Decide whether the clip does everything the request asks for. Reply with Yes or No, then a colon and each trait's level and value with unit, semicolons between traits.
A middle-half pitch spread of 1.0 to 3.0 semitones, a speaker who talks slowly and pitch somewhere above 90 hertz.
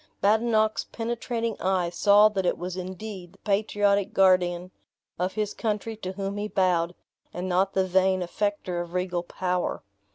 No: narrow, 2.5 semitones; average, 155 wpm; high, 190 Hz